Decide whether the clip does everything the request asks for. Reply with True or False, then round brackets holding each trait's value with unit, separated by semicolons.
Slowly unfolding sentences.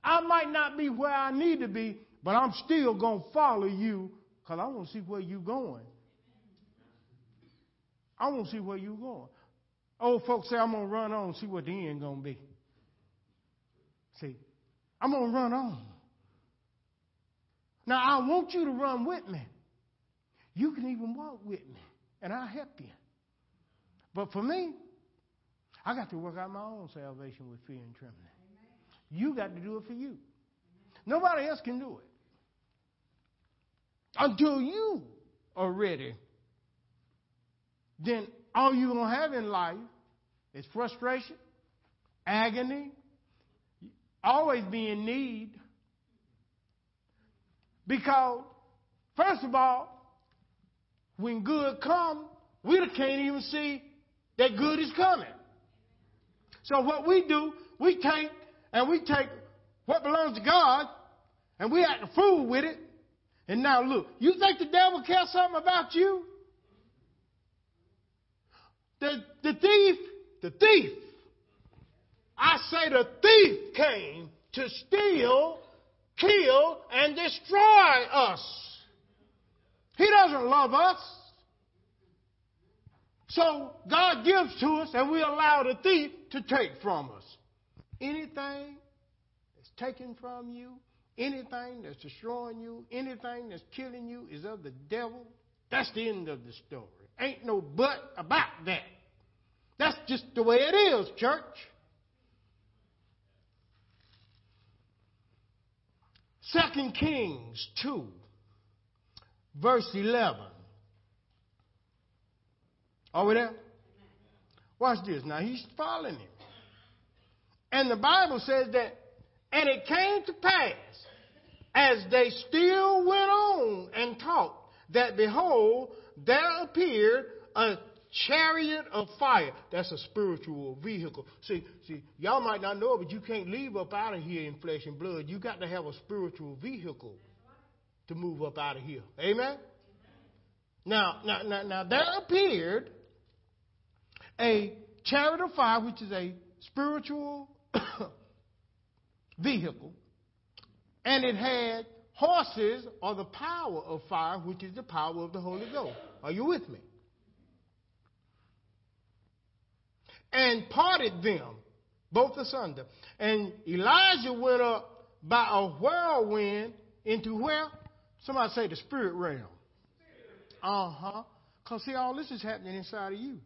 True (130 wpm)